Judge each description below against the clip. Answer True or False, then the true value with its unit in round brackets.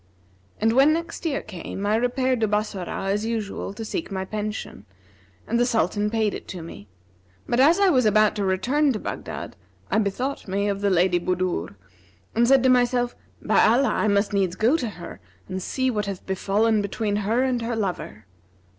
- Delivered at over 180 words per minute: True (190 wpm)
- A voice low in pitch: False (215 Hz)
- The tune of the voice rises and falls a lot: False (3.9 semitones)